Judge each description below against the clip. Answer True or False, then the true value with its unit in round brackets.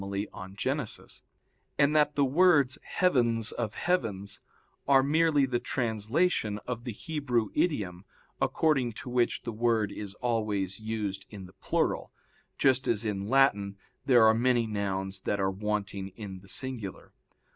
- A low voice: True (115 Hz)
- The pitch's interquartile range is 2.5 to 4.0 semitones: False (4.8 semitones)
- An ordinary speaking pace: True (145 wpm)